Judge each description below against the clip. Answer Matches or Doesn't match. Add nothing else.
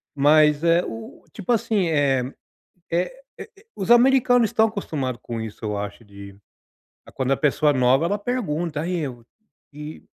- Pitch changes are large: Matches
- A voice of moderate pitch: Matches